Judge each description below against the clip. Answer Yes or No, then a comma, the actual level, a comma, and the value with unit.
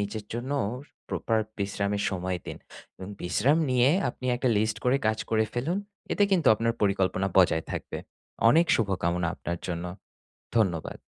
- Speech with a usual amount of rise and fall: Yes, average, 4.6 semitones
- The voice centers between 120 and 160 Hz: No, low, 105 Hz